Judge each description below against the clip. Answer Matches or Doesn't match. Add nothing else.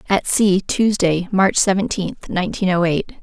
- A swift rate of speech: Doesn't match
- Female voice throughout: Matches